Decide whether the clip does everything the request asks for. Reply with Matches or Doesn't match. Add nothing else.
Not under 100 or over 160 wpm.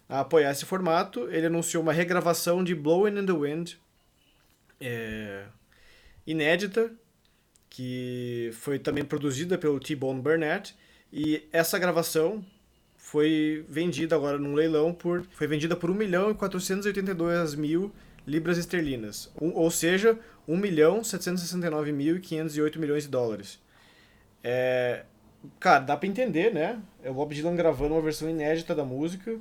Matches